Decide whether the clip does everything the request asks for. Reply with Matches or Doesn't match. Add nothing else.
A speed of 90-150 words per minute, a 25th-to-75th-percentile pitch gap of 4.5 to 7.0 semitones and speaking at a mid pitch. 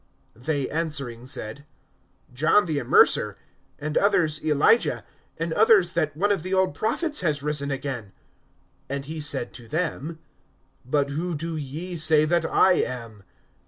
Doesn't match